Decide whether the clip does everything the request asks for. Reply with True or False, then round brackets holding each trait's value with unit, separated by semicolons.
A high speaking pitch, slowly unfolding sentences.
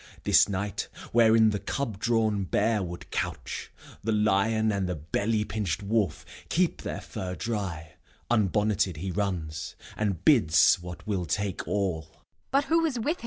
False (100 Hz; 130 wpm)